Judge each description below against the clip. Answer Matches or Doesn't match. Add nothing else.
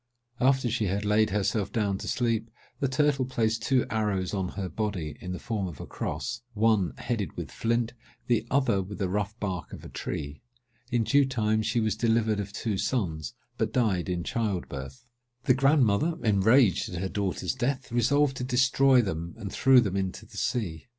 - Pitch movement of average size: Matches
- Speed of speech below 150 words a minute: Doesn't match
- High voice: Doesn't match